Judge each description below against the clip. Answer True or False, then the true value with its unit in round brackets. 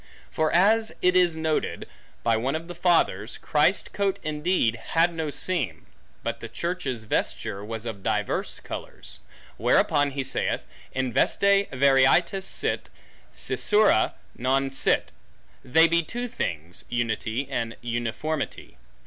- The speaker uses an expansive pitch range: True (6.7 semitones)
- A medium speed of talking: False (130 wpm)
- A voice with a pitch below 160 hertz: True (140 Hz)